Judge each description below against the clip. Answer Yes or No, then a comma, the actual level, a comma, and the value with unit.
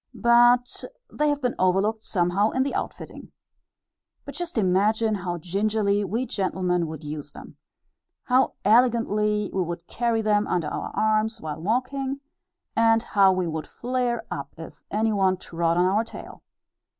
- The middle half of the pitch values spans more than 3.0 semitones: Yes, average, 4.6 semitones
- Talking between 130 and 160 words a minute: Yes, average, 150 wpm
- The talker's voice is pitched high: Yes, high, 210 Hz